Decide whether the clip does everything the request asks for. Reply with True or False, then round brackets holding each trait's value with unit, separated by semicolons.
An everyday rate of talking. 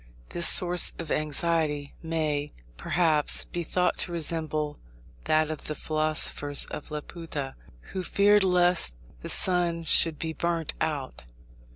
False (130 wpm)